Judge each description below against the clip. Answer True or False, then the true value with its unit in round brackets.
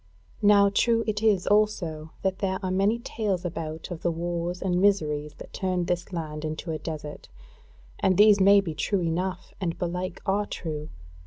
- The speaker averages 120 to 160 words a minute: False (175 wpm)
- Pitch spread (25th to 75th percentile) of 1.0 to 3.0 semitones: False (3.5 semitones)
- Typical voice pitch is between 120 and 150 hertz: False (180 Hz)